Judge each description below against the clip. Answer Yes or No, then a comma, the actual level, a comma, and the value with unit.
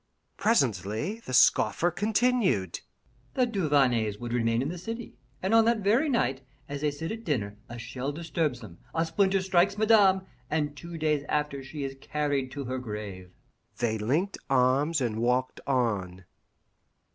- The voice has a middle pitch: Yes, medium, 145 Hz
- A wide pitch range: Yes, wide, 7.7 semitones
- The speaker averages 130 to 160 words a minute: Yes, average, 155 wpm